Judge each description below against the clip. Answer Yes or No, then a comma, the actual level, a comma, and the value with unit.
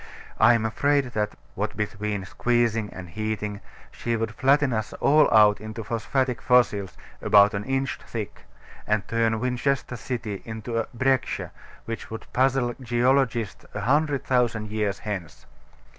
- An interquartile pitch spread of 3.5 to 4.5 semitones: No, average, 3.1 semitones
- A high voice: No, low, 115 Hz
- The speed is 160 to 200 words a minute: No, average, 145 wpm